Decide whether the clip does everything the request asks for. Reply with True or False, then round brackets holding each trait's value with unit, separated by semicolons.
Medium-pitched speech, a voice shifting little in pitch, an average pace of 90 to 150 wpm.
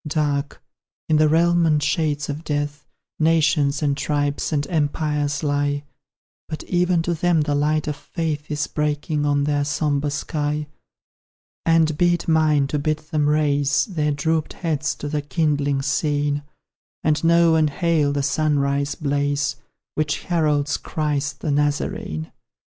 True (150 Hz; 1.5 semitones; 145 wpm)